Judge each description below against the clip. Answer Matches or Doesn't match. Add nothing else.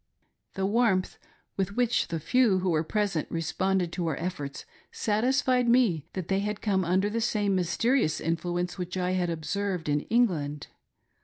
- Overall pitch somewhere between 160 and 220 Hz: Matches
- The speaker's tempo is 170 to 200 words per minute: Doesn't match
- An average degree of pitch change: Matches